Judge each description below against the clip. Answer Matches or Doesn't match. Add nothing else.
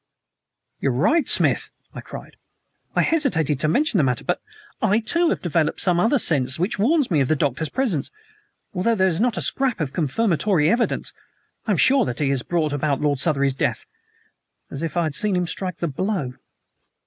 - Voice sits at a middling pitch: Matches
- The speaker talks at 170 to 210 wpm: Matches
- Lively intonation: Matches